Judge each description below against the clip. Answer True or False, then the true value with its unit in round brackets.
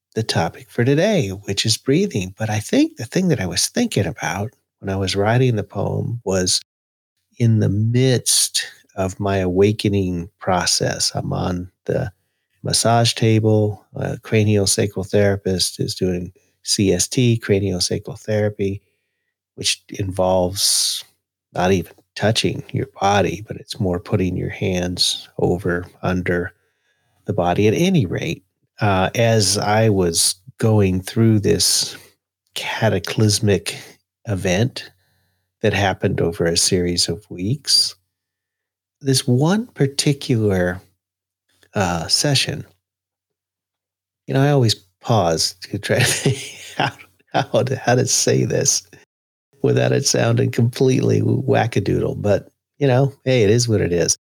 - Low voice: True (105 Hz)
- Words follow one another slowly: True (125 wpm)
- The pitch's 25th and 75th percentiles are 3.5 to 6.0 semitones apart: True (4.5 semitones)